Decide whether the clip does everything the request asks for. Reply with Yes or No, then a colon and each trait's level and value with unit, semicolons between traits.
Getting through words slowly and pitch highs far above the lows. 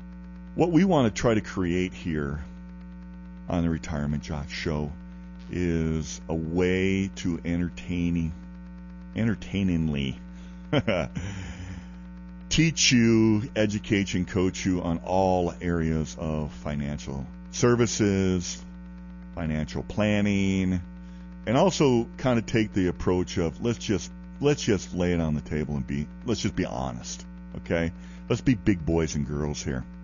Yes: slow, 130 wpm; wide, 7.7 semitones